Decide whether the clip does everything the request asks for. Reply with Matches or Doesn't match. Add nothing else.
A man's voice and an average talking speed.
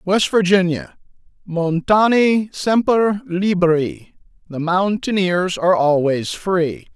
Doesn't match